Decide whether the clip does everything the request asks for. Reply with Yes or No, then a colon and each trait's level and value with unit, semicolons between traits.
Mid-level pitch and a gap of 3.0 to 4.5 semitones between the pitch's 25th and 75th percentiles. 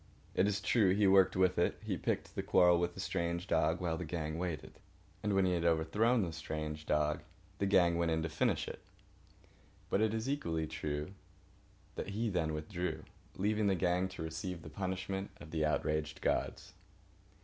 No: very low, 90 Hz; average, 3.4 semitones